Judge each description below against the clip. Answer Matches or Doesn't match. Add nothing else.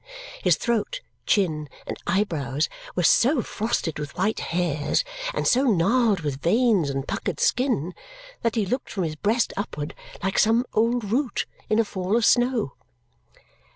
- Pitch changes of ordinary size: Doesn't match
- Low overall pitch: Doesn't match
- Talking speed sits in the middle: Matches